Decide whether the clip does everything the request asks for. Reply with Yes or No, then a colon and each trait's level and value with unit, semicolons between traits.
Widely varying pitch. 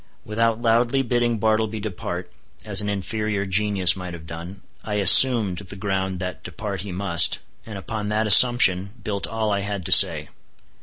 No: average, 2.7 semitones